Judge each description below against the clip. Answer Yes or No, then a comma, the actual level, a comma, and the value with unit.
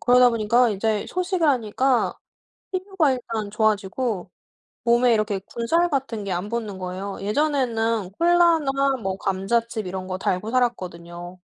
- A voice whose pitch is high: Yes, high, 230 Hz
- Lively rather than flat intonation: No, average, 5.0 semitones